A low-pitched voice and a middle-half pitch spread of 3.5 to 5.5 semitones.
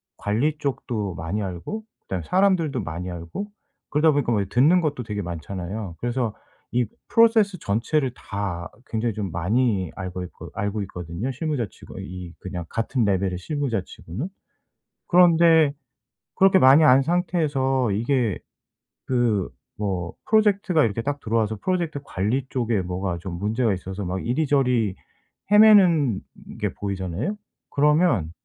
No: low, 115 Hz; wide, 7.7 semitones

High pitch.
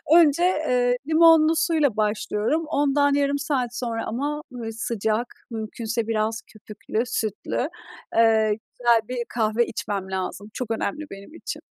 Yes: high, 240 Hz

